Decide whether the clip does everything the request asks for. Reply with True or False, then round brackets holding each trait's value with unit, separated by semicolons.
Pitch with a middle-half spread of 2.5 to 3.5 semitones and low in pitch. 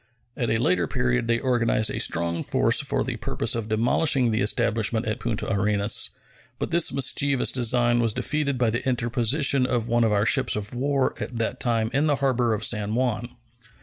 True (2.8 semitones; 120 Hz)